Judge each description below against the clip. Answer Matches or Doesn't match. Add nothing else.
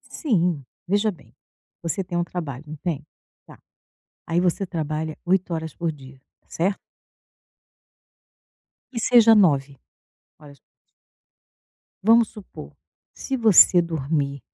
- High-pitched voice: Doesn't match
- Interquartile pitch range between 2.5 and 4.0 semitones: Doesn't match